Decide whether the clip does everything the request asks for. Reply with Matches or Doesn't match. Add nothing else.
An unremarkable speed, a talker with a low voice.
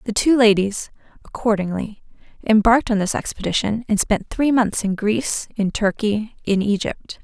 Doesn't match